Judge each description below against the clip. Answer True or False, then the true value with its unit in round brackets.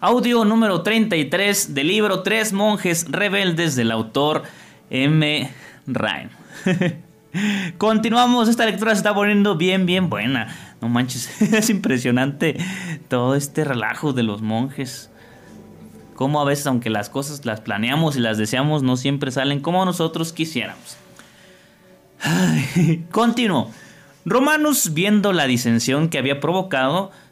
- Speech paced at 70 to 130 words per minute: True (125 wpm)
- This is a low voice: False (160 Hz)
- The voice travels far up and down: True (7.2 semitones)